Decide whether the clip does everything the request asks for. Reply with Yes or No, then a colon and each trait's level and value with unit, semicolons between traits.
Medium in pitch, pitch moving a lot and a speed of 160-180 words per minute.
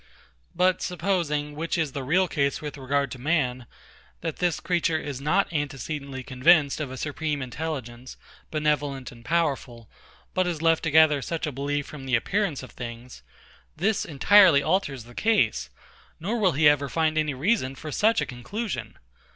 No: medium, 150 Hz; average, 3.8 semitones; average, 165 wpm